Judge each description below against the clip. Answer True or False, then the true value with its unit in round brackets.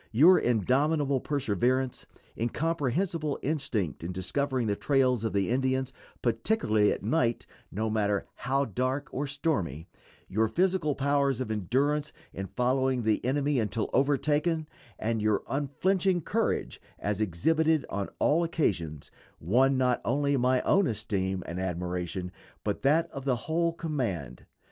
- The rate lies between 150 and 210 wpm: False (135 wpm)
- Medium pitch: False (130 Hz)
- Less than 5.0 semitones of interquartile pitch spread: False (5.6 semitones)